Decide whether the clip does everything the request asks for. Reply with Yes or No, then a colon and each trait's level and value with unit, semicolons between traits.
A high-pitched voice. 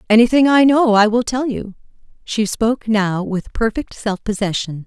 Yes: high, 225 Hz